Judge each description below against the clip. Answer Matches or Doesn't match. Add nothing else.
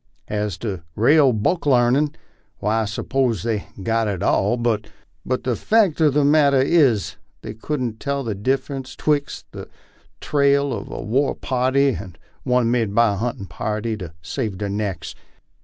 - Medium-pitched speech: Doesn't match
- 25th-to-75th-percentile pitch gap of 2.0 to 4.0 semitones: Doesn't match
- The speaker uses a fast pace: Doesn't match